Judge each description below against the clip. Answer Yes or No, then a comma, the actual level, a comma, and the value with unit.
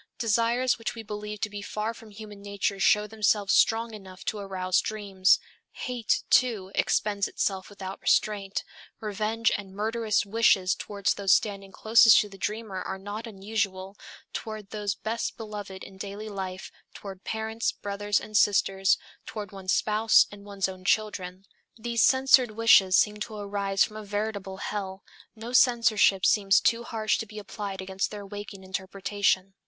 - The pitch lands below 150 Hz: No, high, 205 Hz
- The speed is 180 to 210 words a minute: No, average, 160 wpm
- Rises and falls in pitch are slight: Yes, narrow, 2.0 semitones